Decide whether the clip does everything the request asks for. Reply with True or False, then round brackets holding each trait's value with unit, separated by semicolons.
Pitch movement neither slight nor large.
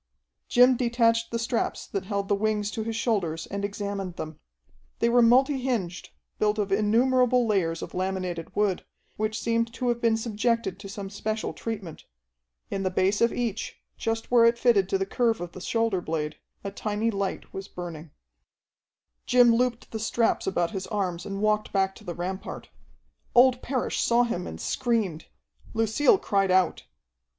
True (3.3 semitones)